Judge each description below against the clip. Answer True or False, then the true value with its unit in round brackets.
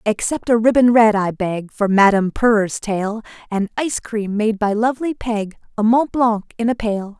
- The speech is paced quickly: False (190 wpm)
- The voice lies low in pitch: False (220 Hz)